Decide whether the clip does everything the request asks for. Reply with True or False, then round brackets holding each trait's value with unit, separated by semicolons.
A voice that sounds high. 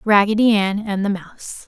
True (205 Hz)